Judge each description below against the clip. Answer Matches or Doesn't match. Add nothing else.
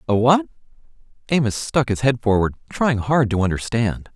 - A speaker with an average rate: Matches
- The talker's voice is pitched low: Matches